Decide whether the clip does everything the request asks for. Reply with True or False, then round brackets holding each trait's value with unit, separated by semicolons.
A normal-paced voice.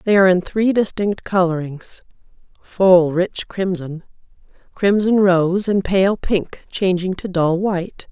False (125 wpm)